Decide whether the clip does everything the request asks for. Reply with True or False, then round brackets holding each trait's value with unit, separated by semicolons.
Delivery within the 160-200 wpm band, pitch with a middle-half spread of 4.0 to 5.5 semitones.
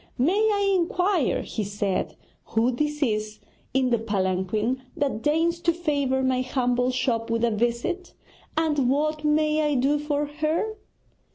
False (150 wpm; 4.6 semitones)